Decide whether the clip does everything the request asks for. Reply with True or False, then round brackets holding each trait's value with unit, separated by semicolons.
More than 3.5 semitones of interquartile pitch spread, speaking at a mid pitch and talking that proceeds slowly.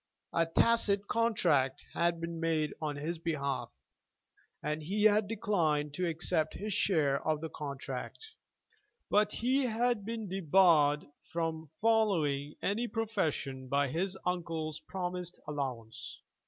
True (5.5 semitones; 165 Hz; 125 wpm)